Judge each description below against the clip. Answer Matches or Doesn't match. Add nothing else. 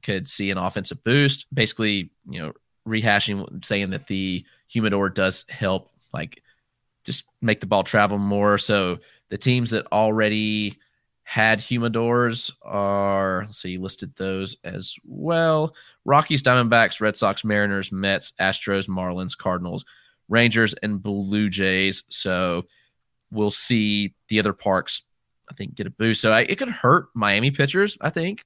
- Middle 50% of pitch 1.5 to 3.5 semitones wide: Matches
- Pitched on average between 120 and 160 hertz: Doesn't match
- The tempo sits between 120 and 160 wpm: Matches